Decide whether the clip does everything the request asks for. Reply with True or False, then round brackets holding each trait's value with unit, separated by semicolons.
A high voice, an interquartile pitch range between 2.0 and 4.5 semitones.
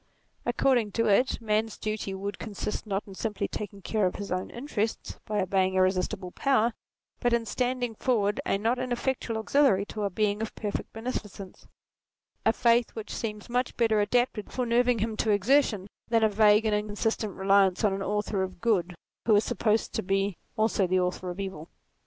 True (210 Hz; 2.8 semitones)